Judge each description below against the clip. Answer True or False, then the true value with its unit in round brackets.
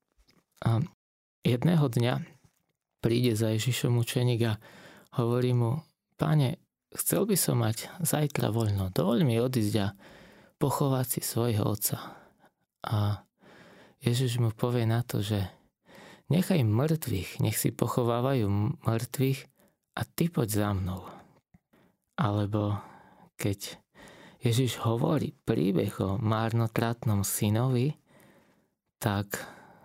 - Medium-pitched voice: False (120 Hz)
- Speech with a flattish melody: False (4.6 semitones)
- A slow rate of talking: True (105 wpm)